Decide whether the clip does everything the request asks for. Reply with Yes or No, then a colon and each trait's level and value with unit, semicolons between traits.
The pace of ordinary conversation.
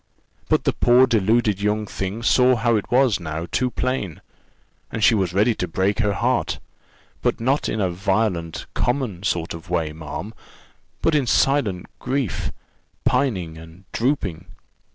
Yes: average, 155 wpm